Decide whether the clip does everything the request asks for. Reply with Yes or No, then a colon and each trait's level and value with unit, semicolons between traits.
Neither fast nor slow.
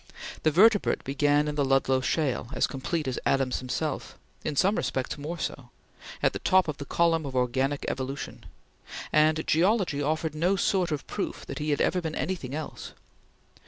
Yes: average, 175 wpm